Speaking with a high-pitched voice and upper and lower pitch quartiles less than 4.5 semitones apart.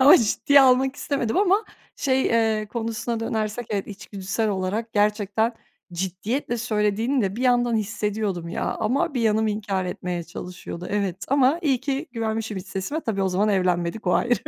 Yes: high, 220 Hz; average, 3.7 semitones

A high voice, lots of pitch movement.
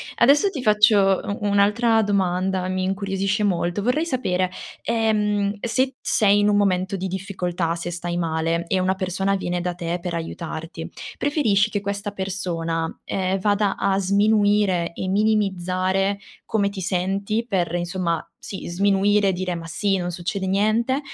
No: high, 195 Hz; narrow, 2.5 semitones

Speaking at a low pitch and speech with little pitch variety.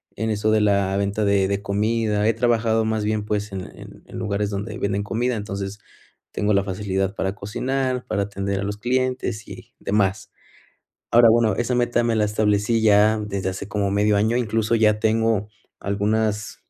Yes: low, 105 Hz; narrow, 1.9 semitones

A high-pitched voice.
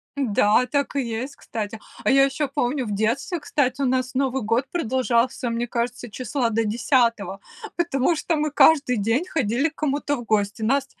Yes: very high, 255 Hz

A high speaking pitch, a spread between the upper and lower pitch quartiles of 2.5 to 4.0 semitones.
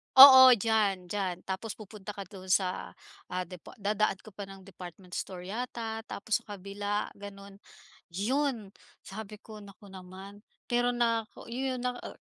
Yes: high, 205 Hz; average, 2.9 semitones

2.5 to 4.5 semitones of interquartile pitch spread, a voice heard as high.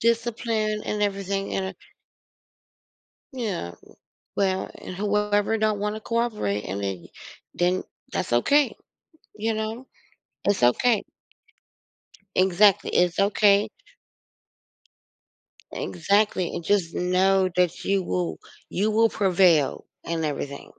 Yes: average, 3.4 semitones; high, 195 Hz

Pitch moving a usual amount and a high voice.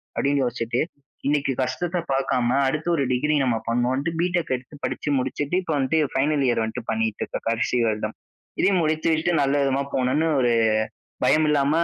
No: average, 3.7 semitones; low, 135 Hz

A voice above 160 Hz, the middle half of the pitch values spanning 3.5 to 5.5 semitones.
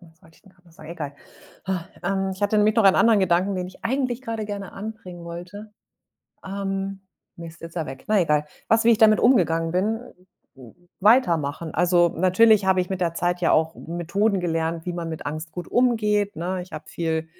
Yes: medium, 185 Hz; average, 3.8 semitones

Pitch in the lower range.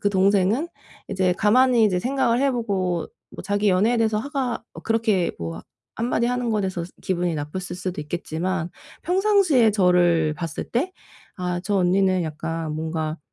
No: high, 190 Hz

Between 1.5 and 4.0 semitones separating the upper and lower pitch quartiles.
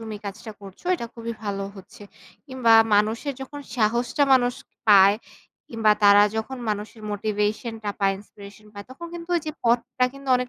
Yes: average, 3.5 semitones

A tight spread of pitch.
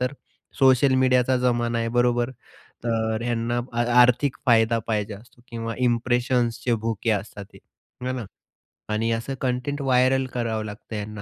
Yes: narrow, 1.8 semitones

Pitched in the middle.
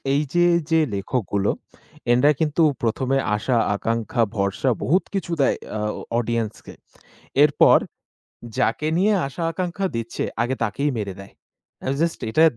No: low, 130 Hz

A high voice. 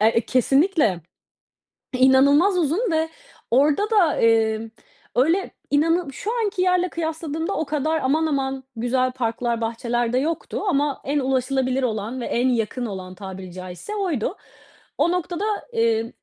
Yes: very high, 270 Hz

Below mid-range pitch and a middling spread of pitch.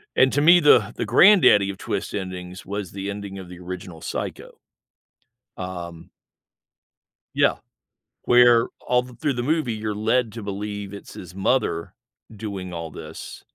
Yes: low, 105 Hz; average, 4.7 semitones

